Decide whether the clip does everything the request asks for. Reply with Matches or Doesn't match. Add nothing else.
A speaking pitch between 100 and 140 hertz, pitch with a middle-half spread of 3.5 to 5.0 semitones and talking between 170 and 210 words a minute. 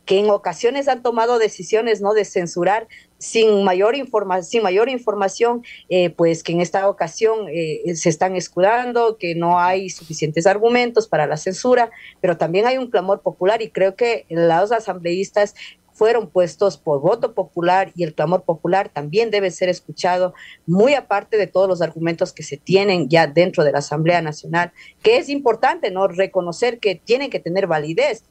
Doesn't match